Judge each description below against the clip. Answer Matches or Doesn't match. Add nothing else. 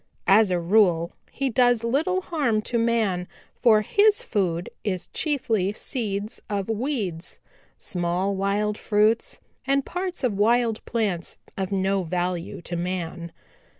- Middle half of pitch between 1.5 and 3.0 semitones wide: Doesn't match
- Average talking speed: Doesn't match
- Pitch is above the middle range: Matches